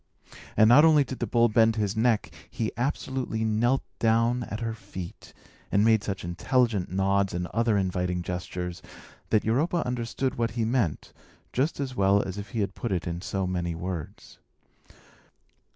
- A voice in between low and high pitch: No, low, 110 Hz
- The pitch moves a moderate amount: Yes, average, 4.1 semitones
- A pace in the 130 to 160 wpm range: No, average, 170 wpm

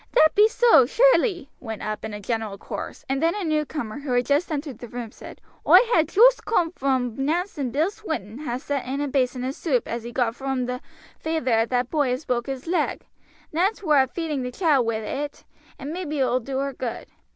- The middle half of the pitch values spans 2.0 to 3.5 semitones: No, average, 4.5 semitones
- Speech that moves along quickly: Yes, fast, 225 wpm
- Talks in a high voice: Yes, very high, 275 Hz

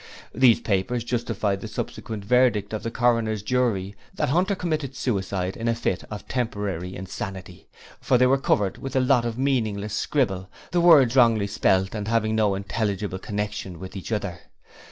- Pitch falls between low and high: No, low, 110 Hz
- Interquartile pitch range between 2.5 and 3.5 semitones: No, average, 4.1 semitones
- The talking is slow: No, average, 170 wpm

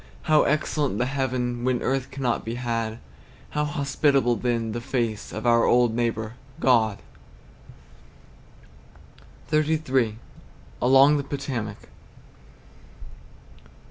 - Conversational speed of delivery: No, slow, 100 wpm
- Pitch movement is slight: No, average, 3.0 semitones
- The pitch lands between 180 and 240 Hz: No, low, 125 Hz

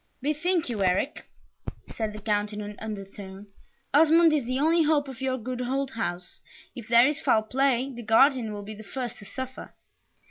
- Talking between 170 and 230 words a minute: Yes, average, 185 wpm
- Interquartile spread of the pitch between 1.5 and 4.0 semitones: No, average, 4.5 semitones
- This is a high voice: Yes, high, 245 Hz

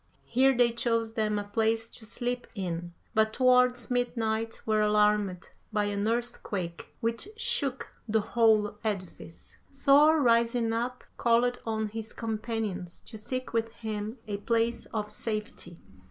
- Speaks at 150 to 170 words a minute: No, average, 140 wpm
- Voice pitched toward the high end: Yes, high, 225 Hz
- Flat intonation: Yes, narrow, 2.3 semitones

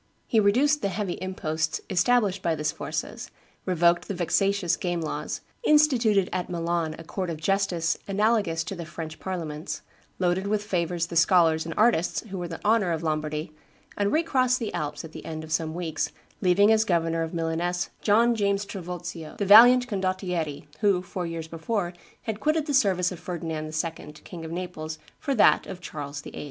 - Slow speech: No, average, 180 wpm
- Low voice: No, medium, 180 Hz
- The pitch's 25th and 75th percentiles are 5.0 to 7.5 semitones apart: No, average, 3.8 semitones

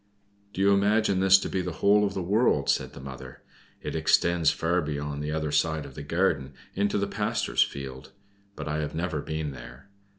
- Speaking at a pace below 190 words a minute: No, average, 200 wpm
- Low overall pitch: Yes, very low, 80 Hz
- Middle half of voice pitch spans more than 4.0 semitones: Yes, average, 4.8 semitones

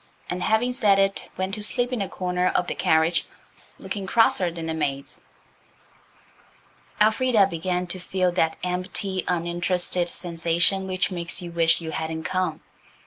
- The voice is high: No, medium, 180 Hz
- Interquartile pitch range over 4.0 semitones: No, narrow, 2.4 semitones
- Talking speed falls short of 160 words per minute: Yes, average, 150 wpm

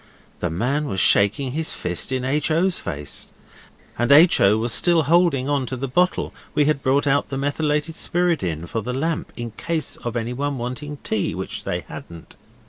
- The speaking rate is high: No, average, 190 wpm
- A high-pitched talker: No, low, 135 Hz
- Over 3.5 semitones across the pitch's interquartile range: Yes, average, 4.5 semitones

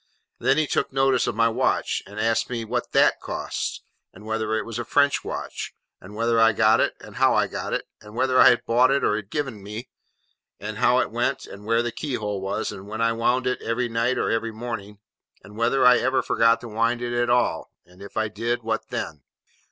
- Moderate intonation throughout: No, narrow, 2.2 semitones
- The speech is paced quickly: Yes, fast, 230 wpm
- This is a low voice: Yes, low, 115 Hz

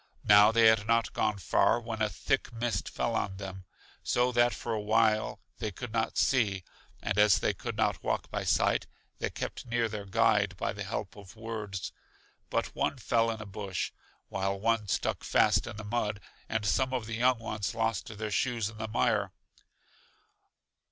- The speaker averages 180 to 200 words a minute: Yes, average, 185 wpm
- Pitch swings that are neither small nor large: No, narrow, 1.9 semitones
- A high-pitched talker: No, low, 110 Hz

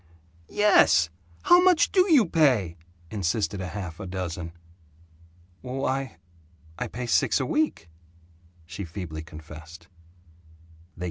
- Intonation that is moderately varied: No, wide, 8.3 semitones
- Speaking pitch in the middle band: No, low, 100 Hz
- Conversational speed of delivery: No, slow, 110 wpm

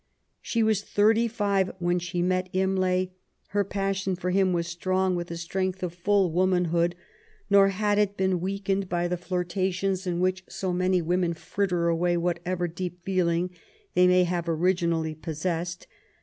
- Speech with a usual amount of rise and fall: No, narrow, 1.7 semitones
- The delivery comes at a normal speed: Yes, average, 165 wpm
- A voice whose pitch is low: No, medium, 180 Hz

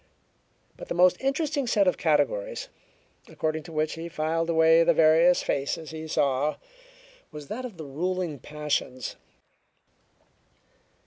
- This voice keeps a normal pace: No, slow, 130 wpm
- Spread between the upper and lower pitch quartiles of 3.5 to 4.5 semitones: No, average, 3.1 semitones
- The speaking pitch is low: No, medium, 165 Hz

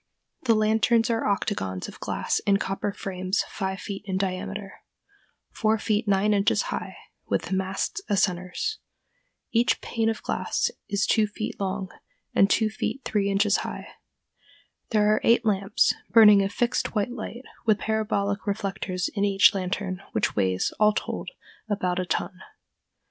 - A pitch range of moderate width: No, narrow, 2.1 semitones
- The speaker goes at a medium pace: Yes, average, 155 wpm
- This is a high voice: Yes, high, 200 Hz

